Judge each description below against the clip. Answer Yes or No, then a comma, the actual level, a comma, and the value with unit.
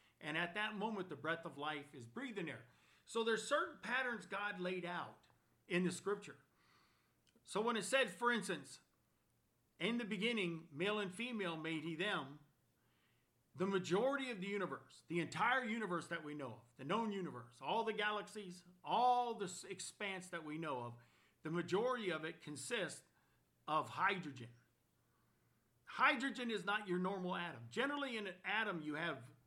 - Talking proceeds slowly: No, average, 165 wpm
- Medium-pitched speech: Yes, medium, 180 Hz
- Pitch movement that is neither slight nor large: No, wide, 6.3 semitones